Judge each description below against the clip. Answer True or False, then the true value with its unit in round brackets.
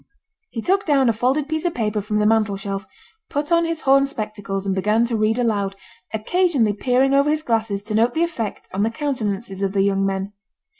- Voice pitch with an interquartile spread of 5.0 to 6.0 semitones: True (5.4 semitones)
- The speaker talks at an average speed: False (210 wpm)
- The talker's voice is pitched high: True (225 Hz)